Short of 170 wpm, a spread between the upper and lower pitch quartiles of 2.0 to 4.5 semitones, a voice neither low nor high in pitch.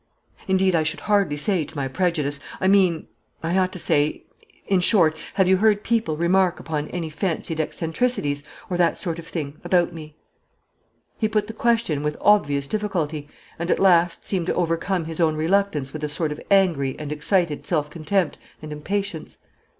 No: average, 180 wpm; average, 3.9 semitones; medium, 170 Hz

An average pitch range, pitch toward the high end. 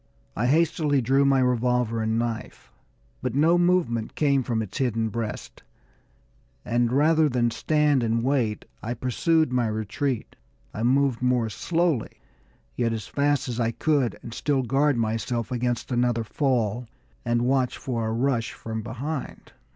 No: average, 3.3 semitones; low, 125 Hz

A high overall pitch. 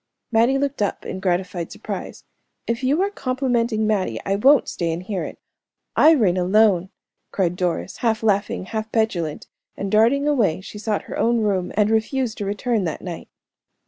Yes: high, 215 Hz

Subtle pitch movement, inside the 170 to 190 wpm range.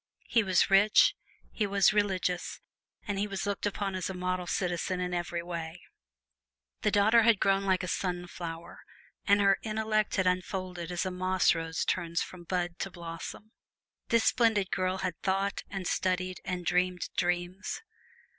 No: narrow, 2.1 semitones; average, 160 wpm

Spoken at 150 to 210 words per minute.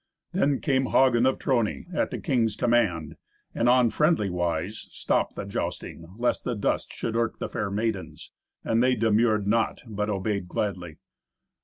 Yes: average, 160 wpm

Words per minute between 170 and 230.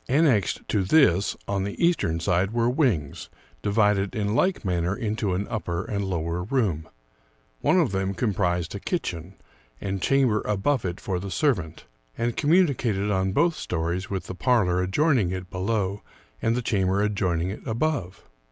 No: average, 160 wpm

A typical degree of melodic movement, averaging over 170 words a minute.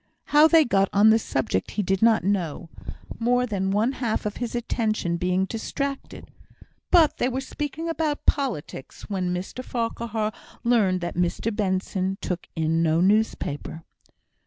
No: average, 5.0 semitones; average, 150 wpm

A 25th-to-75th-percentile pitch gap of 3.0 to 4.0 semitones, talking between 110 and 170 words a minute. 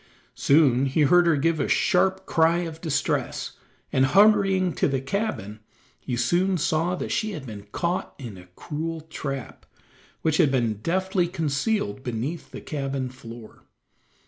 No: average, 5.2 semitones; average, 150 wpm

